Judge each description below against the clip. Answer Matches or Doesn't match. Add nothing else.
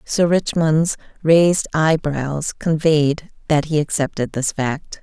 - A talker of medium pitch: Matches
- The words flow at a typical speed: Doesn't match